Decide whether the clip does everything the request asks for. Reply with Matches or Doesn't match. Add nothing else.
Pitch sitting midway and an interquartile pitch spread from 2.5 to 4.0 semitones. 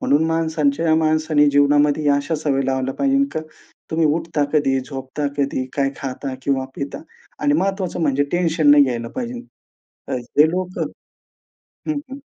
Matches